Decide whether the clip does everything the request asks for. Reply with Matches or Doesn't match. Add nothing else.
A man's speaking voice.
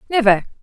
Doesn't match